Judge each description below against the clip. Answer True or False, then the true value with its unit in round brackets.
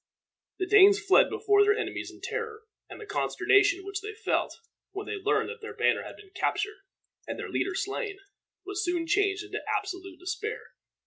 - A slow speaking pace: False (180 wpm)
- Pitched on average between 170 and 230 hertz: False (405 Hz)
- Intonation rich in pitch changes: False (1.5 semitones)